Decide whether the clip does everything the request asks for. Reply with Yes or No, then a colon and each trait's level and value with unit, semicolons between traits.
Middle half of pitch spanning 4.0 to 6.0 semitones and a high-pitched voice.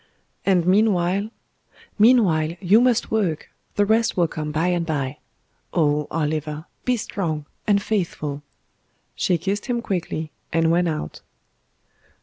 No: average, 4.7 semitones; medium, 175 Hz